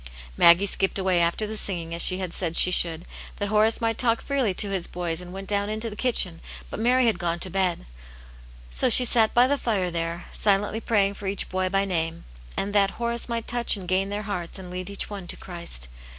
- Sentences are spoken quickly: Yes, fast, 225 wpm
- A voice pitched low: No, high, 195 Hz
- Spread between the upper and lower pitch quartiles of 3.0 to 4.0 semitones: Yes, average, 3.5 semitones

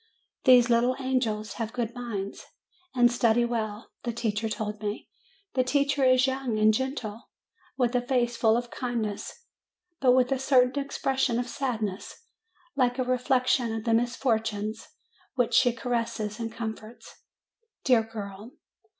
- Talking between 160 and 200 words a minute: No, average, 140 wpm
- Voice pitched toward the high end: Yes, high, 240 Hz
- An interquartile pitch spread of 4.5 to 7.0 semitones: No, narrow, 2.5 semitones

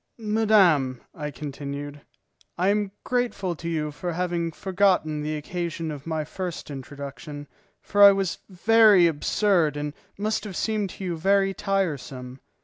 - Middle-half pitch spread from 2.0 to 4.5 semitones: No, average, 5.0 semitones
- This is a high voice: No, medium, 170 Hz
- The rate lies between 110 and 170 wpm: Yes, average, 140 wpm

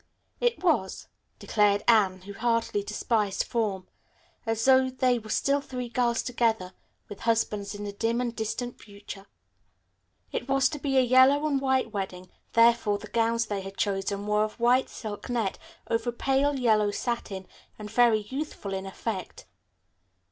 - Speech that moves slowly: No, average, 155 wpm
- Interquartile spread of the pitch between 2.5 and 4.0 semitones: Yes, average, 3.5 semitones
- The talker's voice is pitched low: No, high, 225 Hz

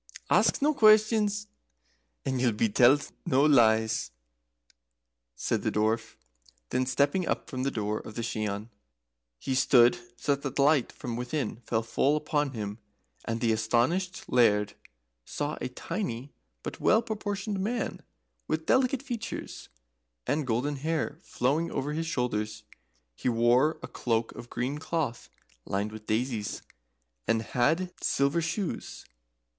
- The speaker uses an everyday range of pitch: No, wide, 6.0 semitones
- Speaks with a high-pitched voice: No, low, 130 Hz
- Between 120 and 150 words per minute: Yes, average, 140 wpm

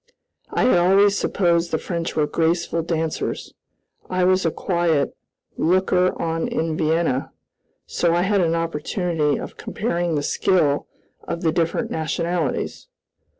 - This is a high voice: No, medium, 170 Hz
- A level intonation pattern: Yes, narrow, 1.9 semitones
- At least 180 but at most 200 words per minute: No, slow, 135 wpm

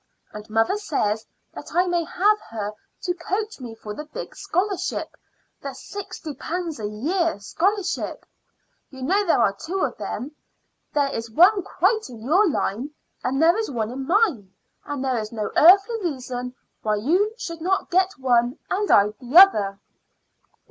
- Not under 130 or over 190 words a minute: Yes, average, 165 wpm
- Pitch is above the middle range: Yes, very high, 300 Hz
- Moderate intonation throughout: No, wide, 8.2 semitones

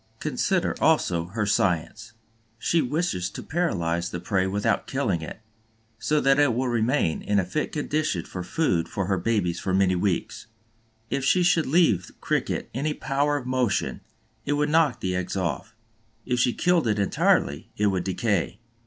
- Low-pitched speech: Yes, low, 110 Hz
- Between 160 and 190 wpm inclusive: Yes, average, 170 wpm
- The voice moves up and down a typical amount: No, wide, 8.1 semitones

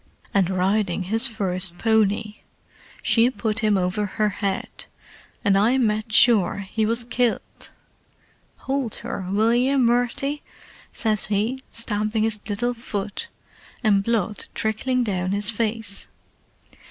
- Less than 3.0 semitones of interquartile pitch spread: Yes, narrow, 2.6 semitones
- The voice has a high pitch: Yes, high, 215 Hz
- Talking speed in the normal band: No, slow, 125 wpm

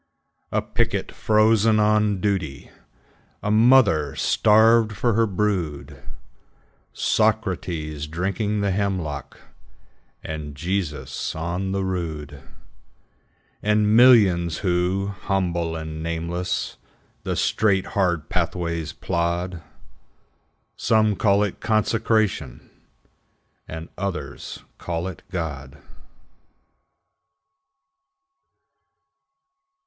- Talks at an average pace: No, slow, 80 wpm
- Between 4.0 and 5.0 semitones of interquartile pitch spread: Yes, average, 4.4 semitones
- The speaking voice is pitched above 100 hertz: No, very low, 95 Hz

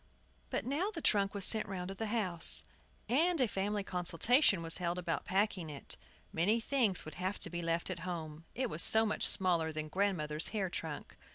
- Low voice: No, medium, 185 Hz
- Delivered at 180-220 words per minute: Yes, average, 200 wpm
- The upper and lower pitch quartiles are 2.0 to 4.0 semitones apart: No, average, 4.5 semitones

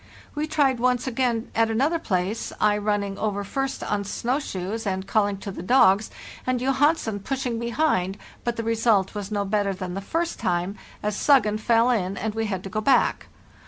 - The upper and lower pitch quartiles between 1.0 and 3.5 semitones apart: No, average, 4.1 semitones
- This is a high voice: Yes, high, 220 Hz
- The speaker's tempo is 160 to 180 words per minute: No, average, 190 wpm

